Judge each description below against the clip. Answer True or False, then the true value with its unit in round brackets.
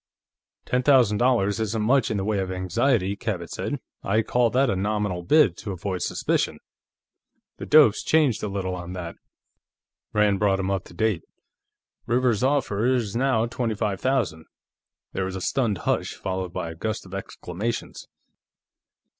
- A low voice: True (105 Hz)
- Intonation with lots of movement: False (4.2 semitones)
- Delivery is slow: False (165 wpm)